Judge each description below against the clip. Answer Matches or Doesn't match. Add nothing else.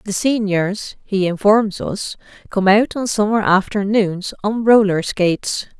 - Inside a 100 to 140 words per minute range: Matches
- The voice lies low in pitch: Doesn't match